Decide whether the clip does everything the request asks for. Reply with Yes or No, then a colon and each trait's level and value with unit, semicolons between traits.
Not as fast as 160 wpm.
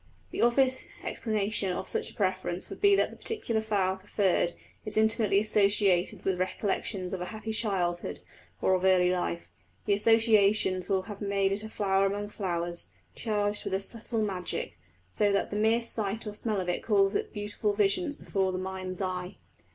No: average, 180 wpm